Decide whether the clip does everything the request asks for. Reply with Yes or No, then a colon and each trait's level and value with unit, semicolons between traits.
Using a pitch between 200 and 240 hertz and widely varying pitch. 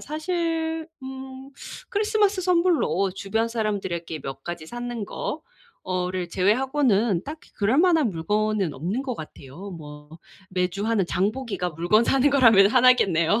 Yes: high, 215 Hz; wide, 6.9 semitones